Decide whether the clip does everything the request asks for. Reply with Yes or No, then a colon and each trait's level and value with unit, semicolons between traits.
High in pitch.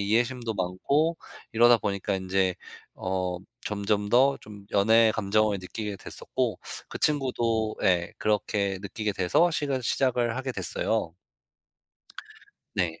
No: low, 105 Hz